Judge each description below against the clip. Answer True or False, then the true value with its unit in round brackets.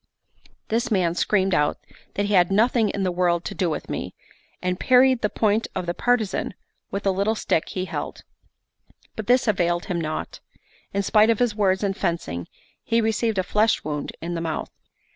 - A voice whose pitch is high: True (195 Hz)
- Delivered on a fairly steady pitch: False (4.0 semitones)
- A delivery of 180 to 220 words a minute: True (190 wpm)